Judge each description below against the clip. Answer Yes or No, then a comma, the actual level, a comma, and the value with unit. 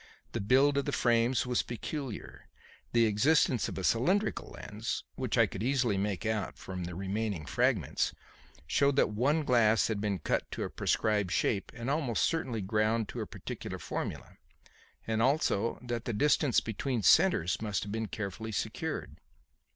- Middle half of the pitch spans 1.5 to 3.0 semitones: No, average, 3.7 semitones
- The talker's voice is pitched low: Yes, low, 115 Hz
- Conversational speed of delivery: Yes, average, 165 wpm